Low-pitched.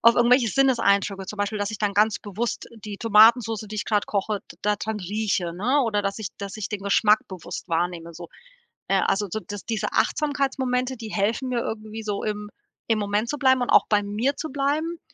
No: high, 215 Hz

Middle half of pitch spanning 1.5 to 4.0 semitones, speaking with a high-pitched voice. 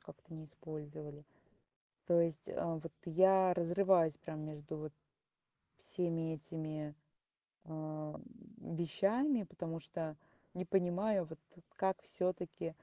No: average, 2.9 semitones; medium, 165 Hz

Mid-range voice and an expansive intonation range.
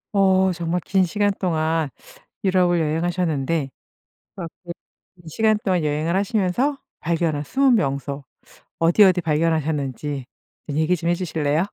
No: medium, 170 Hz; average, 3.4 semitones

